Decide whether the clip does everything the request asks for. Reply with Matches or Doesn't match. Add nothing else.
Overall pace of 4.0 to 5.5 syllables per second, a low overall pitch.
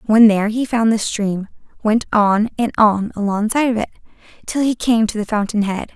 Doesn't match